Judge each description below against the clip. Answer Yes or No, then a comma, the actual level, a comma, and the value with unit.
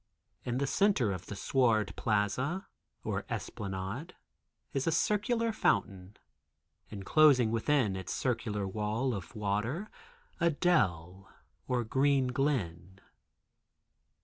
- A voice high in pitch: No, low, 115 Hz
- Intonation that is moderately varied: No, wide, 6.5 semitones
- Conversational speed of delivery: No, slow, 105 wpm